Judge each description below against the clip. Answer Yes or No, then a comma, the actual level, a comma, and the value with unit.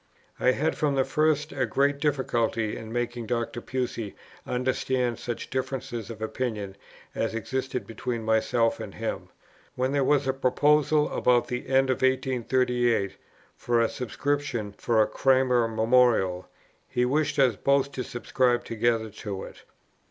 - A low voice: Yes, low, 125 Hz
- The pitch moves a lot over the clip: No, narrow, 2.6 semitones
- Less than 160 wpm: Yes, average, 145 wpm